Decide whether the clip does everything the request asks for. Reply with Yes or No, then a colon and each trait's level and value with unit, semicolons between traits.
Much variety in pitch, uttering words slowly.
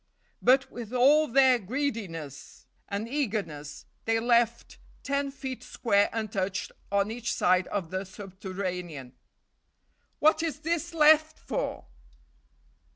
Yes: wide, 6.7 semitones; slow, 105 wpm